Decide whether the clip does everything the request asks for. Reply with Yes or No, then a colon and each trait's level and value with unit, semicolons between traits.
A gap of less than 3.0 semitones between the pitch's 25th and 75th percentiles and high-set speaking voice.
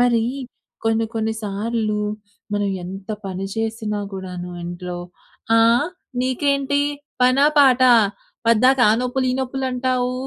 No: average, 3.8 semitones; high, 230 Hz